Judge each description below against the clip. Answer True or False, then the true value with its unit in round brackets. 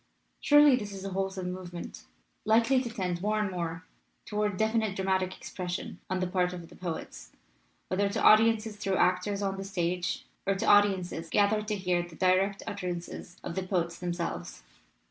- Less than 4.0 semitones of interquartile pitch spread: True (2.6 semitones)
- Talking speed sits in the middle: True (170 wpm)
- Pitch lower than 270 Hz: True (190 Hz)